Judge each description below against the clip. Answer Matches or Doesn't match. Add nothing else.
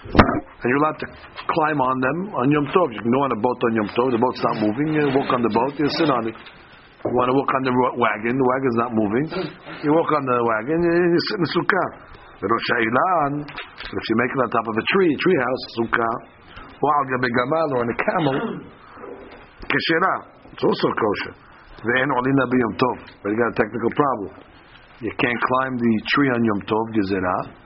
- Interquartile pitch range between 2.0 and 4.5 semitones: Matches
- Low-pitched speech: Matches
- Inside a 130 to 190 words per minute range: Doesn't match